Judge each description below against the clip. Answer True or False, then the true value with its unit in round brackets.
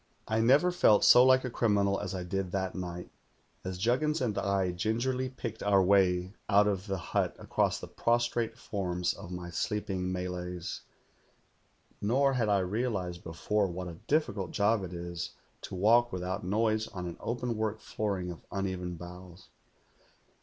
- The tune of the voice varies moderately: True (3.8 semitones)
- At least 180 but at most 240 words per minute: False (160 wpm)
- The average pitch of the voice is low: True (100 Hz)